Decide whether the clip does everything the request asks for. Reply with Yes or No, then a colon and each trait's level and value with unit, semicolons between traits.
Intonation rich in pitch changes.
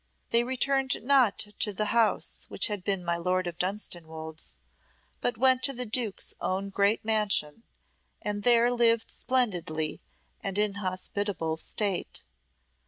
No: average, 4.3 semitones